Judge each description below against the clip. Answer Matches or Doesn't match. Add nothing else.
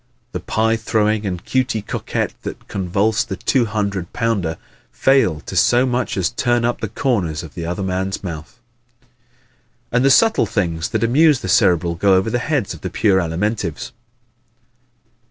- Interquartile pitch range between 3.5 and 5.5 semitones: Matches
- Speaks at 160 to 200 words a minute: Matches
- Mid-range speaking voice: Doesn't match